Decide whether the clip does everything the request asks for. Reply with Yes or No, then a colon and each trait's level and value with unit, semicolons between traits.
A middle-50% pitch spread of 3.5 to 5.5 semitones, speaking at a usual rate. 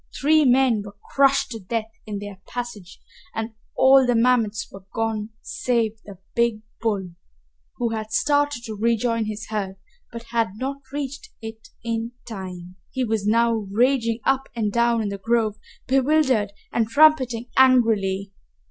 No: average, 3.0 semitones; average, 150 wpm